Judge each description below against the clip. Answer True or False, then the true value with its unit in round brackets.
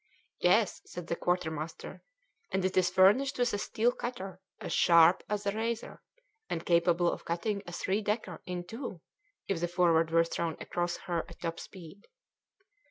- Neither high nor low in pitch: True (180 Hz)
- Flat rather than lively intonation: False (3.3 semitones)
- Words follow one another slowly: False (165 wpm)